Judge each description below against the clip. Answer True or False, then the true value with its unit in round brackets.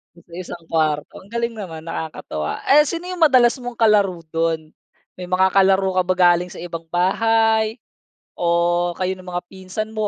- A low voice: False (185 Hz)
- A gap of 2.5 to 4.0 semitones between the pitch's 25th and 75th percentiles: False (4.4 semitones)